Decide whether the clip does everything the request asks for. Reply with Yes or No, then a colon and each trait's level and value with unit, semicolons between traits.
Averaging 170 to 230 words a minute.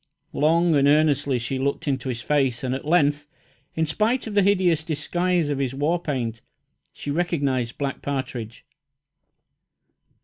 No: average, 145 wpm